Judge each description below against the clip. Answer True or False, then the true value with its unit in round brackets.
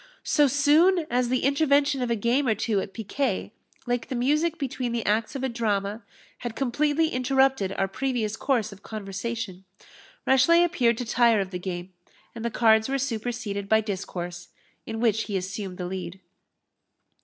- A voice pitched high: True (235 Hz)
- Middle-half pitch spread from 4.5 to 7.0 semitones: True (4.8 semitones)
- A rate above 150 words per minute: True (170 wpm)